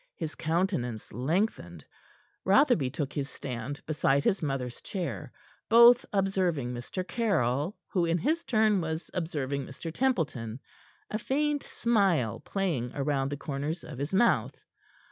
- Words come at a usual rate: No, slow, 130 wpm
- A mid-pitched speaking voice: Yes, medium, 160 Hz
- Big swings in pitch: Yes, wide, 6.5 semitones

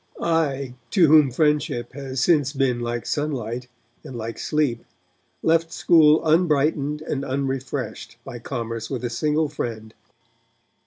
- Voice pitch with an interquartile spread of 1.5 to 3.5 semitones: No, average, 4.0 semitones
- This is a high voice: No, medium, 140 Hz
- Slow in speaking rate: Yes, slow, 125 wpm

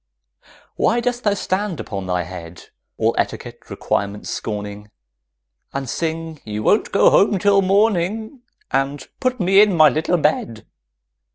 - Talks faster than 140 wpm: No, slow, 135 wpm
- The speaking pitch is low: No, medium, 165 Hz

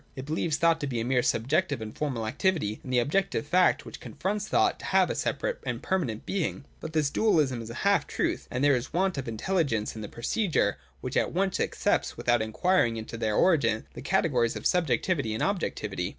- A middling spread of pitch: No, wide, 7.7 semitones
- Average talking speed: No, fast, 210 wpm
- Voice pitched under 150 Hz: Yes, medium, 140 Hz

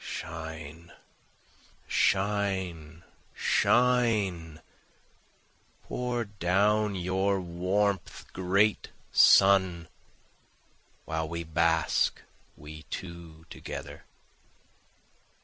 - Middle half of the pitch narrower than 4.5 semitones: Yes, average, 3.6 semitones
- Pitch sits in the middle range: No, very low, 90 Hz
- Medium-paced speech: No, slow, 60 wpm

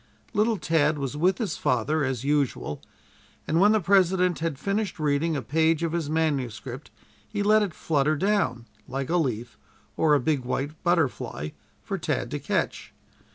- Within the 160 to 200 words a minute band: Yes, average, 165 wpm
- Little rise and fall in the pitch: No, average, 4.6 semitones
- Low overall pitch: No, medium, 155 Hz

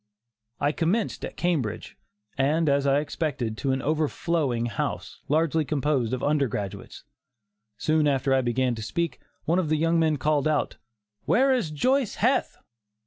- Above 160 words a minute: No, average, 150 wpm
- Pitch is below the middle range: No, medium, 150 Hz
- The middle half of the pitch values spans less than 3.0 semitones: No, average, 3.6 semitones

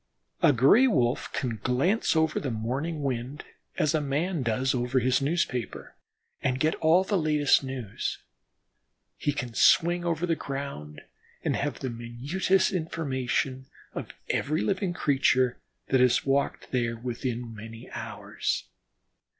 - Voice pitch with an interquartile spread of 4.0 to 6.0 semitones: Yes, average, 4.5 semitones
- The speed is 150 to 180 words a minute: No, slow, 135 wpm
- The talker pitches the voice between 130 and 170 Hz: Yes, low, 135 Hz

